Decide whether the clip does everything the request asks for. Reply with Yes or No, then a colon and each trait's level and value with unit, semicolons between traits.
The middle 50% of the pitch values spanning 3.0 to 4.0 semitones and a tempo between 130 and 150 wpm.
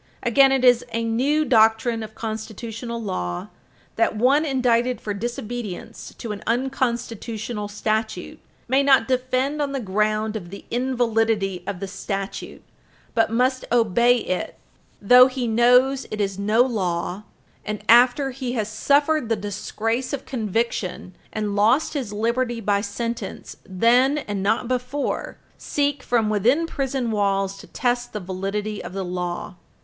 Yes: average, 3.5 semitones; average, 145 wpm